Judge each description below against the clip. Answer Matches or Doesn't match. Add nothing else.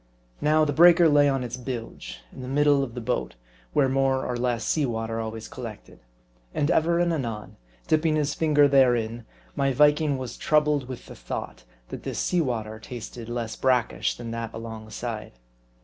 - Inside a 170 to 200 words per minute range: Matches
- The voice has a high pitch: Doesn't match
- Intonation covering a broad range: Doesn't match